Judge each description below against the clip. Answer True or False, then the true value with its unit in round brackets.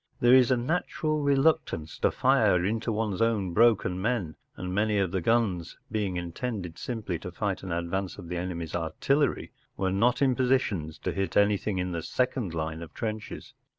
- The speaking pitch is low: True (100 Hz)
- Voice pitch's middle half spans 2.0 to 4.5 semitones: False (5.3 semitones)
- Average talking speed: True (180 wpm)